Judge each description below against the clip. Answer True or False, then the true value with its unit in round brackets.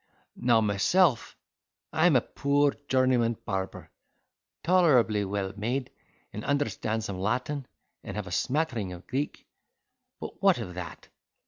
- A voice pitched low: True (120 Hz)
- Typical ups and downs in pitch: False (5.7 semitones)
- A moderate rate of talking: False (130 wpm)